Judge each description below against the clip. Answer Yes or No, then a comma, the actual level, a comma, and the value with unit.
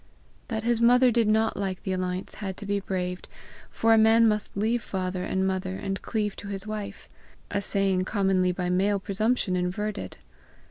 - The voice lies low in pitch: No, high, 200 Hz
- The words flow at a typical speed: Yes, average, 180 wpm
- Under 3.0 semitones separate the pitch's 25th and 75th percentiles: Yes, narrow, 2.6 semitones